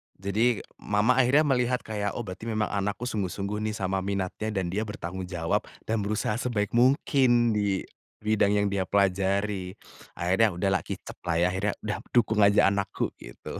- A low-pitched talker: Yes, low, 105 Hz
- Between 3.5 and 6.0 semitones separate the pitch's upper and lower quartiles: No, narrow, 2.4 semitones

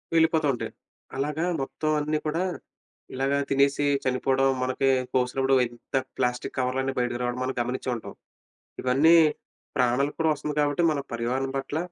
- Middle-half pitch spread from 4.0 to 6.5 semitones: No, narrow, 2.6 semitones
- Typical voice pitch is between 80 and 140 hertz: Yes, low, 135 Hz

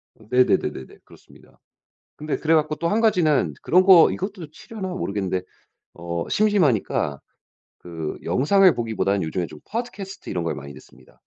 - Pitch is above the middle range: No, medium, 150 Hz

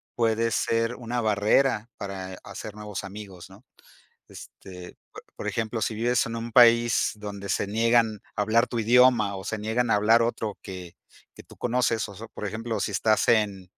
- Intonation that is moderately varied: No, narrow, 2.3 semitones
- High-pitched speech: No, low, 110 Hz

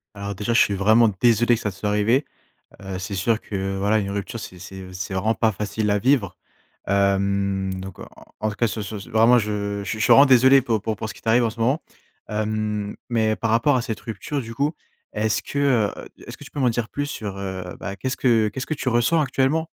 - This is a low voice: Yes, low, 110 Hz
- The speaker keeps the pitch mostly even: No, average, 3.2 semitones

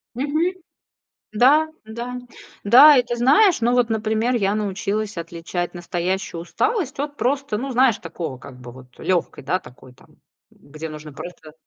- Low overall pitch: No, high, 215 Hz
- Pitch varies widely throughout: Yes, wide, 7.2 semitones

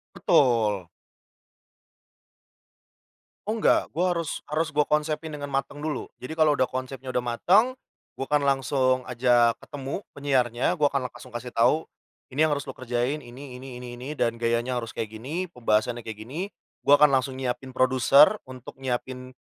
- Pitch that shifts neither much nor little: Yes, average, 3.2 semitones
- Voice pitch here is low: Yes, low, 130 Hz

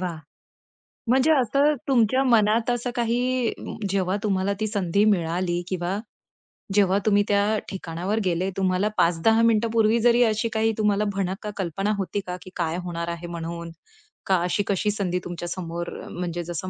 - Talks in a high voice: Yes, high, 195 Hz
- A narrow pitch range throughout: No, average, 4.1 semitones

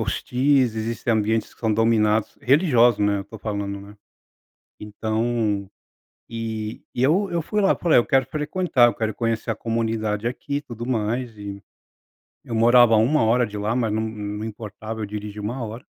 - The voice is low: Yes, low, 115 Hz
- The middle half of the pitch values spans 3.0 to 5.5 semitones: No, narrow, 2.4 semitones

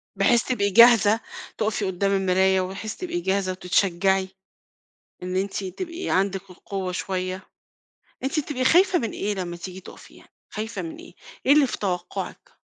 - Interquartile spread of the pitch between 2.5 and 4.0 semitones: No, average, 4.4 semitones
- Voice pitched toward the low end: No, high, 195 Hz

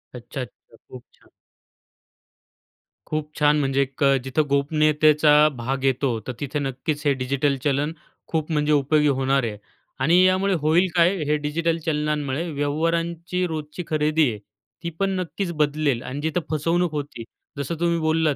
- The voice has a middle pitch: Yes, medium, 150 Hz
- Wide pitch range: No, average, 2.7 semitones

